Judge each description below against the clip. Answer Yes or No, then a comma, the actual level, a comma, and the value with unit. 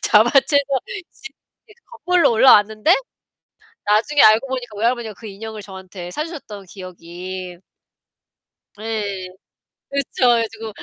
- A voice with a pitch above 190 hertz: Yes, high, 220 Hz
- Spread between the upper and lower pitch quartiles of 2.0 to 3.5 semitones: No, average, 5.1 semitones